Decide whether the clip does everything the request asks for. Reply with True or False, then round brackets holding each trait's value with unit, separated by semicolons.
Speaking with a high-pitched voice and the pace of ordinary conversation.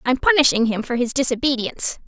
True (255 Hz; 175 wpm)